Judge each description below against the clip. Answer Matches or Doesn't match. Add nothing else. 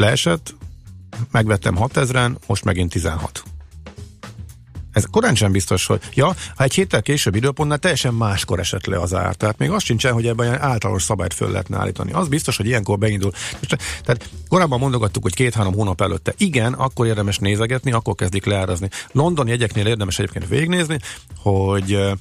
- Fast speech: Matches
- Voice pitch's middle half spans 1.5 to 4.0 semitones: Doesn't match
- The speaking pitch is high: Doesn't match